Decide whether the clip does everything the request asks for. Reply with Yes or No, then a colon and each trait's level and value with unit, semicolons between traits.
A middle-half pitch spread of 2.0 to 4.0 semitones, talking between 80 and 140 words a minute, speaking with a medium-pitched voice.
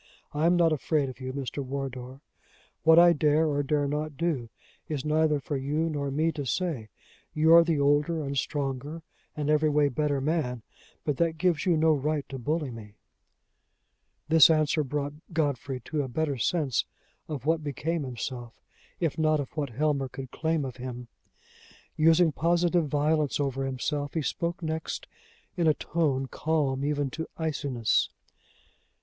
No: average, 2.8 semitones; average, 165 wpm; medium, 150 Hz